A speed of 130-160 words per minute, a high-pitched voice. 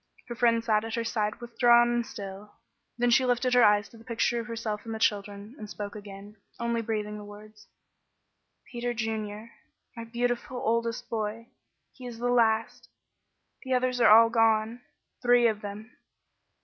No: average, 170 wpm; high, 230 Hz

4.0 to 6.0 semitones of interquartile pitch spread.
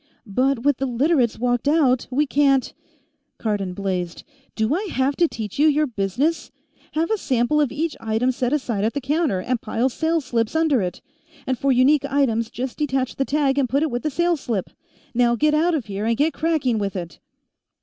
Yes: average, 4.5 semitones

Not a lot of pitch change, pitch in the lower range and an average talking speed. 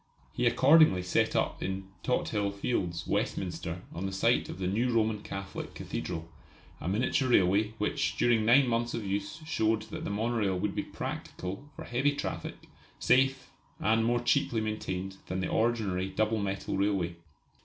No: average, 3.6 semitones; low, 105 Hz; average, 160 wpm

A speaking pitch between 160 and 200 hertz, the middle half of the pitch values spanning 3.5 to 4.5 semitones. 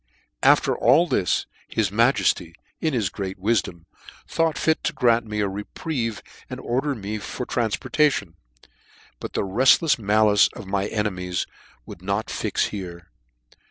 No: low, 105 Hz; average, 4.0 semitones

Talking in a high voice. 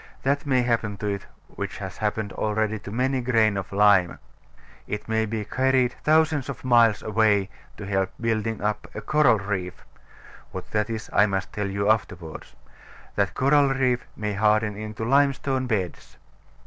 No: low, 110 Hz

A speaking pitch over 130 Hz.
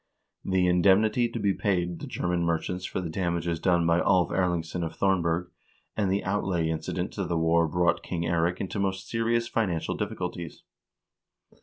No: very low, 90 Hz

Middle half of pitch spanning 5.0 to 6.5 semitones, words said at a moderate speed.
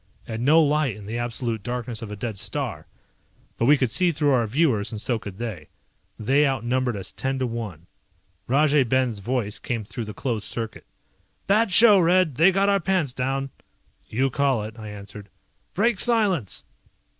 Yes: average, 5.3 semitones; average, 180 wpm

